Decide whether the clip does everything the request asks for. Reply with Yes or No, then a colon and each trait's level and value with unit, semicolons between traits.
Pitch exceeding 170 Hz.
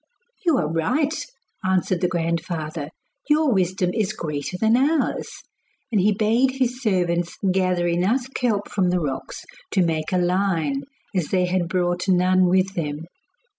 Yes: medium, 185 Hz